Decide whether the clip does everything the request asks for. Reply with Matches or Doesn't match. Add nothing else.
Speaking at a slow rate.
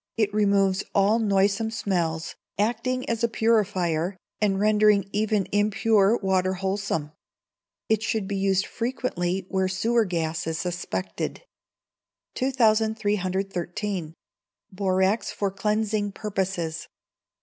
Matches